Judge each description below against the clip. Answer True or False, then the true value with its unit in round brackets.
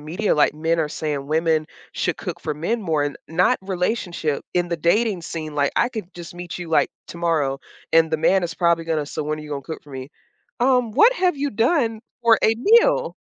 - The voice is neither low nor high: True (170 Hz)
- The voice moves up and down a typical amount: False (6.1 semitones)